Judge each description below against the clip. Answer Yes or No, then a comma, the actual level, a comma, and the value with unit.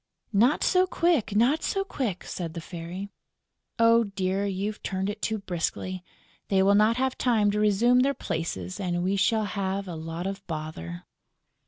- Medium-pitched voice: No, high, 200 Hz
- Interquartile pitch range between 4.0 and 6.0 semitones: Yes, average, 4.3 semitones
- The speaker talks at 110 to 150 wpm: No, average, 170 wpm